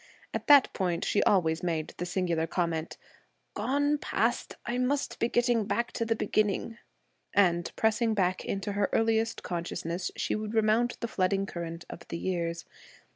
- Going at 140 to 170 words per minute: Yes, average, 160 wpm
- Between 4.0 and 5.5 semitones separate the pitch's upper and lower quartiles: Yes, average, 4.8 semitones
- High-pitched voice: Yes, high, 200 Hz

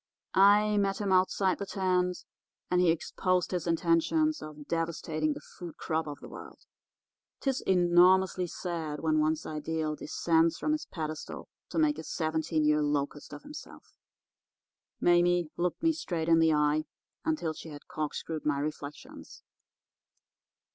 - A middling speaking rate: Yes, average, 145 wpm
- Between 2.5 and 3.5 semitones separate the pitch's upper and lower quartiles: Yes, average, 3.1 semitones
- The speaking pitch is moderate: Yes, medium, 165 Hz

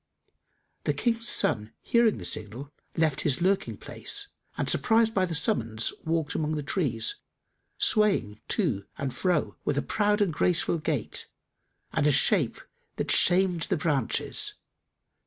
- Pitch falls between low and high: Yes, medium, 160 Hz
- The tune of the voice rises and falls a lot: Yes, wide, 6.4 semitones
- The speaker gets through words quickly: No, average, 140 wpm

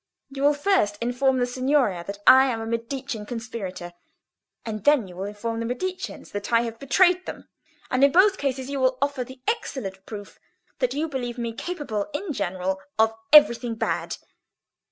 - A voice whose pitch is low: No, high, 245 Hz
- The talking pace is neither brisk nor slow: Yes, average, 175 wpm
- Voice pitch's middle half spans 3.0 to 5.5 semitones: Yes, average, 4.2 semitones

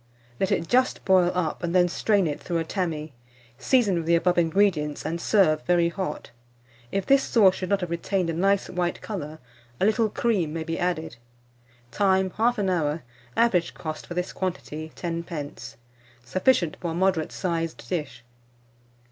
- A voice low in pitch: No, medium, 175 Hz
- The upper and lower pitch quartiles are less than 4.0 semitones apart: Yes, average, 2.9 semitones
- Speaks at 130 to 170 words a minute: Yes, average, 165 wpm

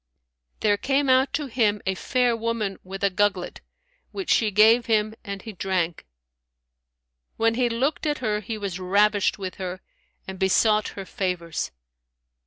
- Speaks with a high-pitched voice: Yes, high, 210 Hz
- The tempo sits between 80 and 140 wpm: No, average, 155 wpm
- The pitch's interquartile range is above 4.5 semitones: No, average, 3.3 semitones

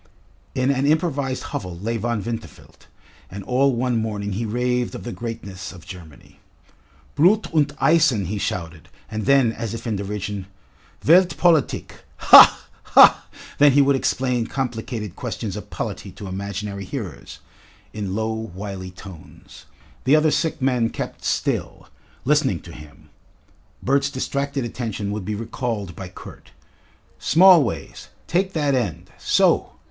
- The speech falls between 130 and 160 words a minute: Yes, average, 140 wpm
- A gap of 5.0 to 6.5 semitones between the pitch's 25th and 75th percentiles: Yes, wide, 5.5 semitones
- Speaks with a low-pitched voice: Yes, low, 115 Hz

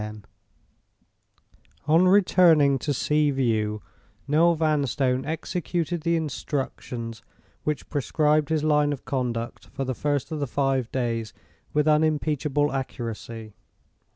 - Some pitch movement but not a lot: Yes, average, 3.3 semitones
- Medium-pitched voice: Yes, medium, 145 Hz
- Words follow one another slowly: Yes, slow, 110 wpm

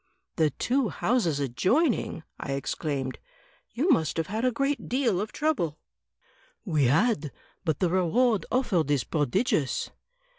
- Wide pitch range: Yes, wide, 8.8 semitones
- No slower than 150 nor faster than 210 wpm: No, slow, 135 wpm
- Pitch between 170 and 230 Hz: Yes, medium, 185 Hz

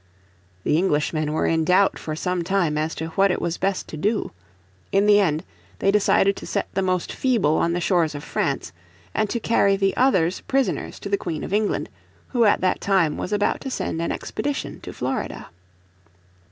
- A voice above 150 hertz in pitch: Yes, medium, 185 Hz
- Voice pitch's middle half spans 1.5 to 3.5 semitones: No, average, 3.9 semitones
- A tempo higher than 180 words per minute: Yes, average, 195 wpm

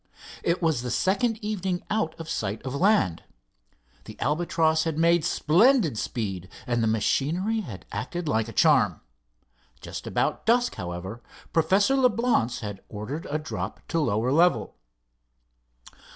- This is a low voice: No, medium, 155 Hz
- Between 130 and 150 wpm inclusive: Yes, slow, 135 wpm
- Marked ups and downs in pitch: Yes, wide, 8.3 semitones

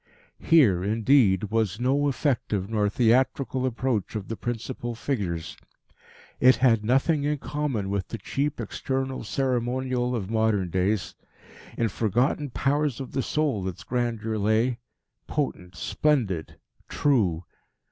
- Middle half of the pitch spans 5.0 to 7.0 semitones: No, average, 4.2 semitones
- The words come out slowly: Yes, slow, 125 wpm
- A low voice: Yes, low, 120 Hz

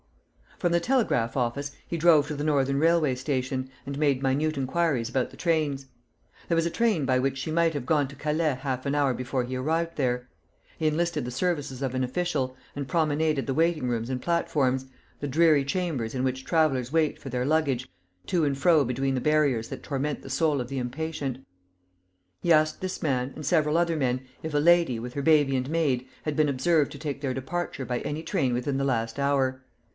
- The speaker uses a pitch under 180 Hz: Yes, medium, 140 Hz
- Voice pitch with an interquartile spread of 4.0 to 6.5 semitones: No, average, 3.4 semitones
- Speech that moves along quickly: Yes, fast, 210 wpm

